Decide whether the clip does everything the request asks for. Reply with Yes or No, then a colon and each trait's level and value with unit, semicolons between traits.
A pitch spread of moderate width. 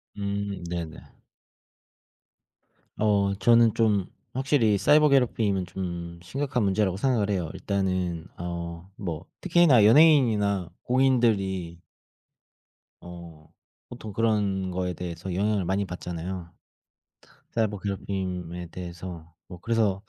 Yes: average, 3.8 semitones